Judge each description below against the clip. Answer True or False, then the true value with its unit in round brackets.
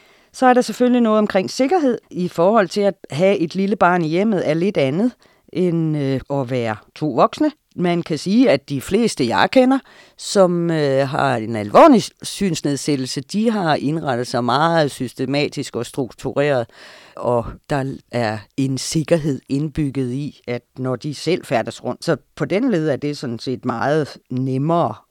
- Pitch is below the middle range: False (150 Hz)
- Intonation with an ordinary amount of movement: False (6.2 semitones)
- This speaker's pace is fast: False (170 wpm)